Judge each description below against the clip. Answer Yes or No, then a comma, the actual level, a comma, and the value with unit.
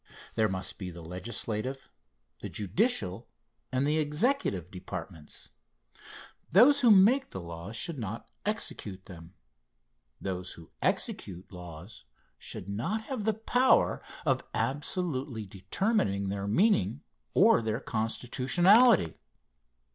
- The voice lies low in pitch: Yes, low, 110 Hz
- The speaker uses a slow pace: Yes, slow, 110 wpm